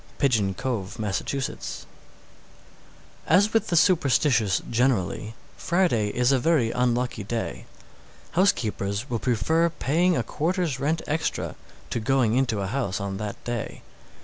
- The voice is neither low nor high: No, low, 125 Hz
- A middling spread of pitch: No, wide, 6.5 semitones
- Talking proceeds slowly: Yes, slow, 130 wpm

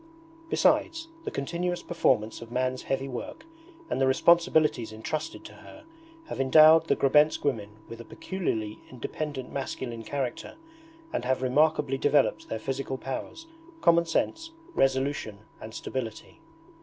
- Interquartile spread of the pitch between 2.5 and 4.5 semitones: Yes, average, 4.1 semitones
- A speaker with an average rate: No, slow, 130 wpm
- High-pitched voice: No, low, 135 Hz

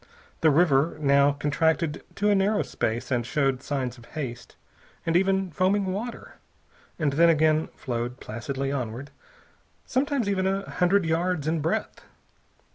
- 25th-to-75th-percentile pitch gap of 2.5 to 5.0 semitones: No, wide, 5.4 semitones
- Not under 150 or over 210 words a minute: No, average, 140 wpm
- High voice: No, medium, 155 Hz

